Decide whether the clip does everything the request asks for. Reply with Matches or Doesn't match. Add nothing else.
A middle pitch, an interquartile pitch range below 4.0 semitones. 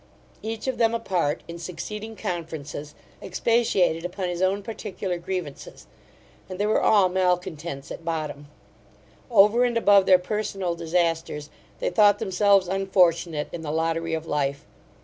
Matches